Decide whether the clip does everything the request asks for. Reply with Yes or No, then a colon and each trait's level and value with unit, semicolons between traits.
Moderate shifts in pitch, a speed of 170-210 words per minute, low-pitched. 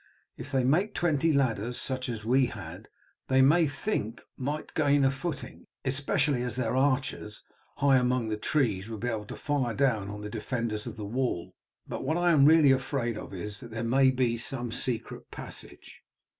Yes: average, 3.7 semitones; average, 190 wpm; low, 130 Hz